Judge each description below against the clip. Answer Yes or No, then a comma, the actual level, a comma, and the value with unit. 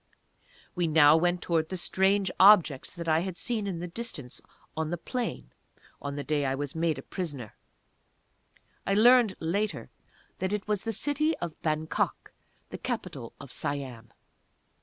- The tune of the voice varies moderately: Yes, average, 4.9 semitones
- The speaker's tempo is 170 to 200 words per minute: No, average, 155 wpm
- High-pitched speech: No, medium, 170 Hz